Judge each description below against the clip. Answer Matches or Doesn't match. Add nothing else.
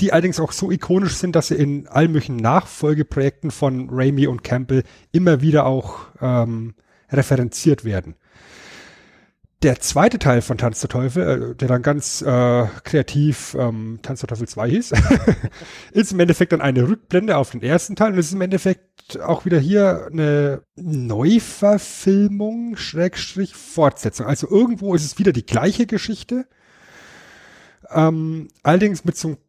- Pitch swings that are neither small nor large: Doesn't match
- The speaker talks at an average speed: Matches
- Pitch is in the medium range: Matches